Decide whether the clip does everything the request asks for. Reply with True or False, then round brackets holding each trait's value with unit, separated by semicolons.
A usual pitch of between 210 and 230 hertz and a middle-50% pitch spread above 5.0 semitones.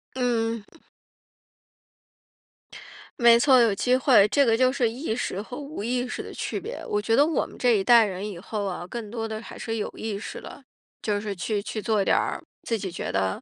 False (225 Hz; 3.2 semitones)